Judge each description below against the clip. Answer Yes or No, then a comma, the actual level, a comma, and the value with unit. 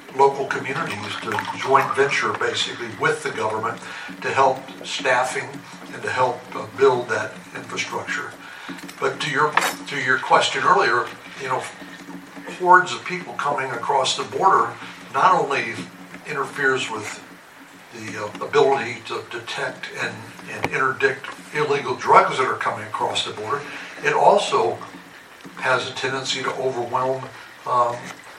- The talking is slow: Yes, slow, 130 wpm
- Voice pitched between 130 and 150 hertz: Yes, medium, 140 Hz